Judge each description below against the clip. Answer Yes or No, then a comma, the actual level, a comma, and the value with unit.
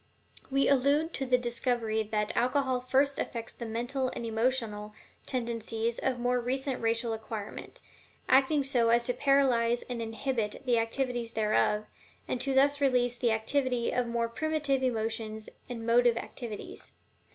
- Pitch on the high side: Yes, high, 245 Hz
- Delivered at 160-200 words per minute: No, average, 150 wpm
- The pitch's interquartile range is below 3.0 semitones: Yes, narrow, 2.6 semitones